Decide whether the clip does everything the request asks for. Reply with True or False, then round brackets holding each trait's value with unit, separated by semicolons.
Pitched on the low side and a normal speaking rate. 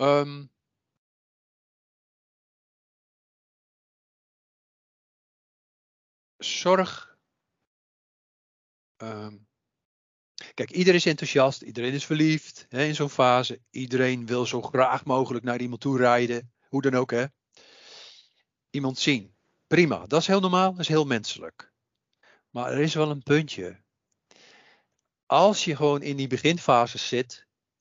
False (130 Hz; 110 wpm)